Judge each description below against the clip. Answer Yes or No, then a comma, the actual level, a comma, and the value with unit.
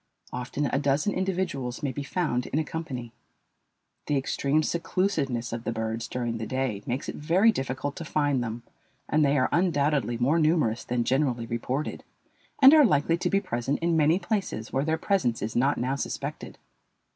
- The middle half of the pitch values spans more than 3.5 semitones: Yes, average, 4.9 semitones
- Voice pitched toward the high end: No, medium, 140 Hz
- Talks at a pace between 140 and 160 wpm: No, average, 180 wpm